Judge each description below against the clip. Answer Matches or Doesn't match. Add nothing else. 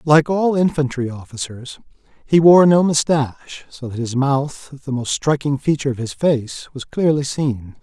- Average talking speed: Matches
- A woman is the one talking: Doesn't match